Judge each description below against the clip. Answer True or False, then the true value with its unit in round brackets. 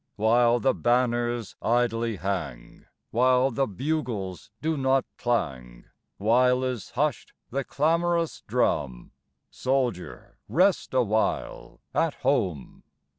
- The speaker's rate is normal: False (100 wpm)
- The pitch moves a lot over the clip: False (4.1 semitones)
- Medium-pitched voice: False (120 Hz)